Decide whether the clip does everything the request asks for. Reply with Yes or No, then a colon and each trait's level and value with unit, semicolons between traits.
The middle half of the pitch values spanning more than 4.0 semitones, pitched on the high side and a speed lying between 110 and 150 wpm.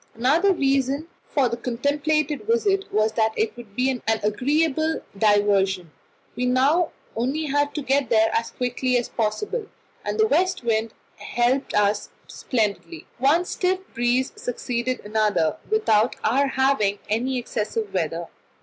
Yes: average, 5.0 semitones; very high, 250 Hz; average, 140 wpm